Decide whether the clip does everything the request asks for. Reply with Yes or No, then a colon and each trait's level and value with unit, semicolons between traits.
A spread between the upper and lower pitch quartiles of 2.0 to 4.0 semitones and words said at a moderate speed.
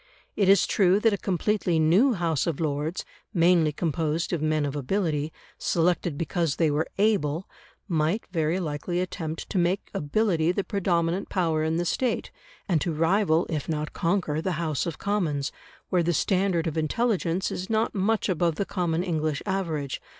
Yes: average, 3.3 semitones; average, 170 wpm